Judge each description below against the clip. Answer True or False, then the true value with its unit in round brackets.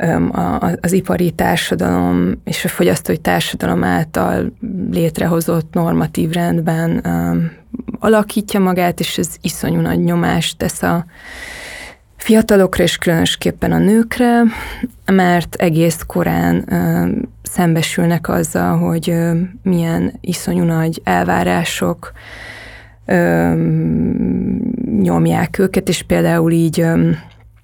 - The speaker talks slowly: True (85 wpm)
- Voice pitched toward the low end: False (170 Hz)